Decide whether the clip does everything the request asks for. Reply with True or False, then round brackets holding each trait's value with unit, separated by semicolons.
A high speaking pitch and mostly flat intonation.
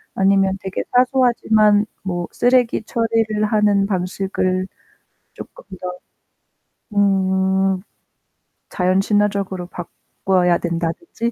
True (195 Hz; 2.3 semitones)